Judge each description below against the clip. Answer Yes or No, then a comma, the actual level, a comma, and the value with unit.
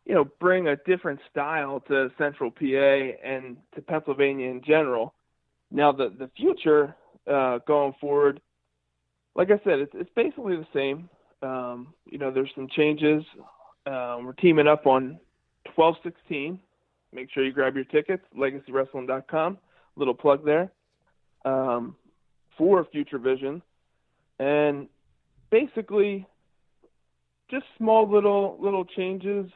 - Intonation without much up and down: No, average, 4.6 semitones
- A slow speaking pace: Yes, slow, 125 wpm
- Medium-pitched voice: Yes, medium, 145 Hz